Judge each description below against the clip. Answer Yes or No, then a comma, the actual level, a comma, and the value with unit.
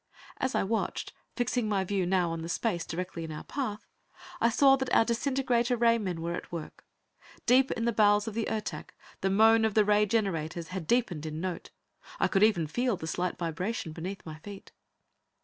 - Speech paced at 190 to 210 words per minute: Yes, average, 200 wpm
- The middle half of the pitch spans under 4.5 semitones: No, average, 5.0 semitones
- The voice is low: No, high, 205 Hz